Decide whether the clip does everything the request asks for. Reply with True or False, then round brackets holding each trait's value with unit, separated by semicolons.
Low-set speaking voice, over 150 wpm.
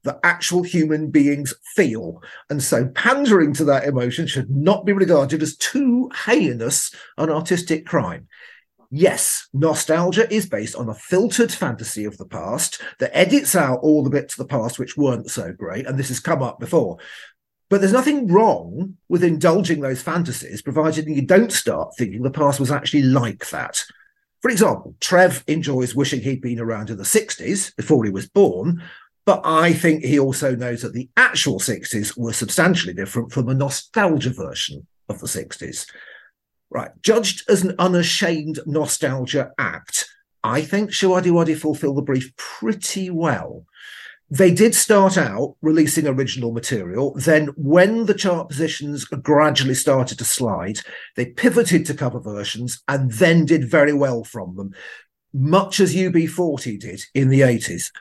False (150 Hz; 160 wpm)